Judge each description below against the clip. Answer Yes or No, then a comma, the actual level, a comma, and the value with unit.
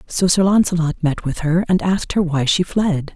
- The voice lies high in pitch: No, medium, 170 Hz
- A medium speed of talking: No, fast, 230 wpm